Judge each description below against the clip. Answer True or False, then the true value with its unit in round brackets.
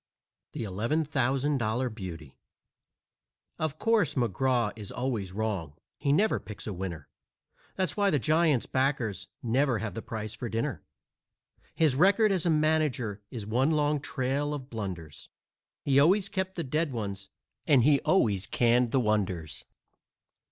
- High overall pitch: False (125 Hz)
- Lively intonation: True (6.0 semitones)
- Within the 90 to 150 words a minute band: True (140 wpm)